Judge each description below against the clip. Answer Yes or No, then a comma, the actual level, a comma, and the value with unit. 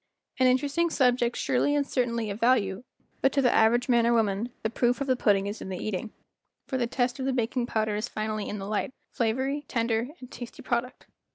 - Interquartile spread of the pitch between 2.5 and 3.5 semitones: Yes, average, 2.8 semitones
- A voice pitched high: Yes, high, 240 Hz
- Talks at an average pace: No, fast, 215 wpm